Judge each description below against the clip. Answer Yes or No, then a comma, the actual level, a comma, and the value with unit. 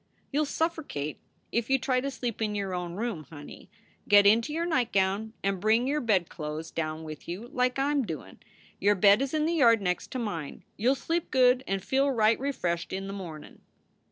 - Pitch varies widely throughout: Yes, wide, 6.6 semitones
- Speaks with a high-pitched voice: Yes, high, 220 Hz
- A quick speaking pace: Yes, fast, 215 wpm